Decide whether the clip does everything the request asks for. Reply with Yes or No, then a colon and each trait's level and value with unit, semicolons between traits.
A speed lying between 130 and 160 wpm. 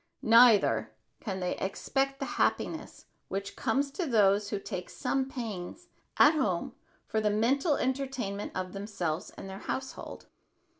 Yes: average, 140 wpm